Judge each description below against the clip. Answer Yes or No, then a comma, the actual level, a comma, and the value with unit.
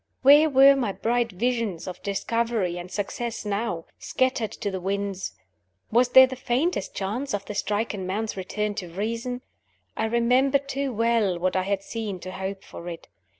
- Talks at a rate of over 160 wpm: Yes, average, 170 wpm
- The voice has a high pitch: Yes, high, 215 Hz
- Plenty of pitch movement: No, average, 4.1 semitones